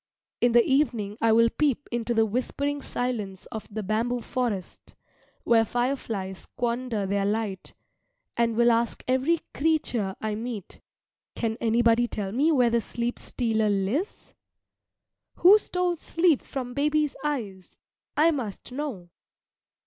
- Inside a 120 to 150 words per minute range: Yes, slow, 135 wpm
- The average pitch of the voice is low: No, high, 235 Hz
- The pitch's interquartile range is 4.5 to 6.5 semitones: No, average, 3.8 semitones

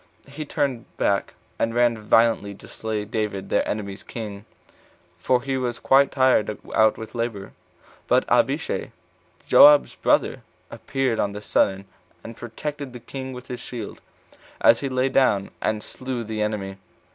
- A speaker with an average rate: Yes, average, 150 wpm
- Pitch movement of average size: Yes, average, 3.6 semitones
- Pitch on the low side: Yes, low, 115 Hz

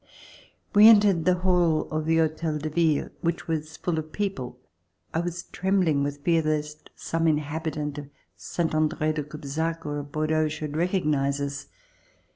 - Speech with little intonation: Yes, narrow, 2.0 semitones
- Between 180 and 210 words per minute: No, average, 165 wpm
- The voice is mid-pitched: Yes, medium, 155 Hz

